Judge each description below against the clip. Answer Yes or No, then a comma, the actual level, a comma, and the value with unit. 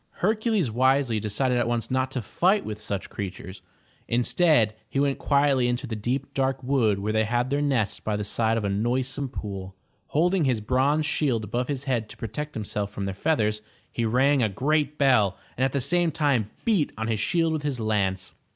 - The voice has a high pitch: No, low, 125 Hz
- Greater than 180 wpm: Yes, average, 200 wpm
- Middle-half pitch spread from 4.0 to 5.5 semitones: Yes, average, 4.7 semitones